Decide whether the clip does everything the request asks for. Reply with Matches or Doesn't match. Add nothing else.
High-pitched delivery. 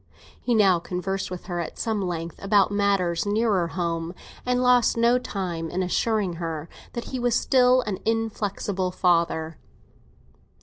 Matches